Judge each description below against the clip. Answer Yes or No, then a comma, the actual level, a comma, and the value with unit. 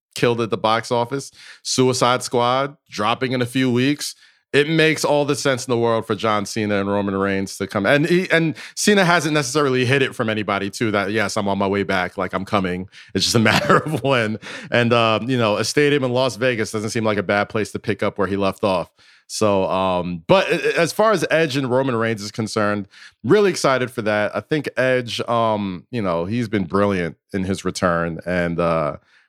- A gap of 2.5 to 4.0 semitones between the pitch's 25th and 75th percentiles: No, average, 4.6 semitones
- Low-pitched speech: Yes, low, 115 Hz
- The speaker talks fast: Yes, fast, 220 wpm